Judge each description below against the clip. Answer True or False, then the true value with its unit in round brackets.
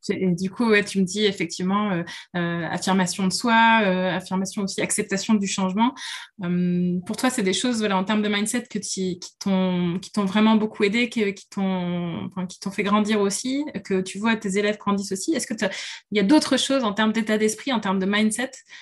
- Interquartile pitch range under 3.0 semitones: True (2.5 semitones)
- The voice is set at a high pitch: True (205 Hz)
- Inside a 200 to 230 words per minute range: True (220 wpm)